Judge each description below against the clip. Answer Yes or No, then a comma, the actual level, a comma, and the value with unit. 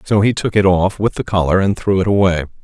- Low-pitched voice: Yes, very low, 95 Hz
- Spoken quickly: Yes, fast, 275 wpm